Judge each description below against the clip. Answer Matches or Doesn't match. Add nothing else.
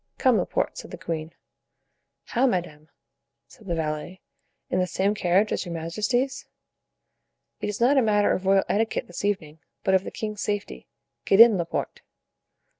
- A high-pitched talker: Matches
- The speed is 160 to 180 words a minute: Matches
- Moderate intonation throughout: Matches